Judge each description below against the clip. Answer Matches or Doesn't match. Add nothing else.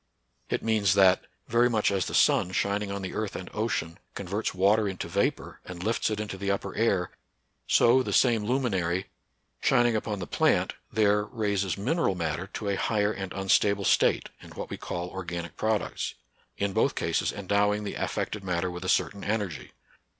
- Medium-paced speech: Matches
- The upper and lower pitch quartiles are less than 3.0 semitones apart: Matches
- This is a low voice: Matches